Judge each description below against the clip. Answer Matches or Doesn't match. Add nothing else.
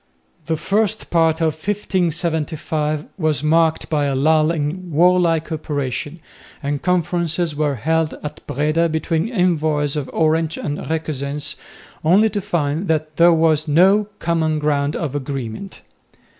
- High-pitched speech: Doesn't match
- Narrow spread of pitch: Matches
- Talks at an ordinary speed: Doesn't match